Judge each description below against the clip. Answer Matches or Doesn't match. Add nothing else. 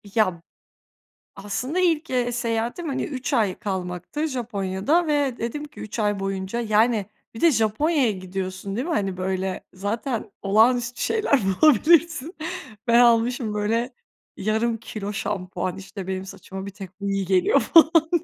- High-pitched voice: Matches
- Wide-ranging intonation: Doesn't match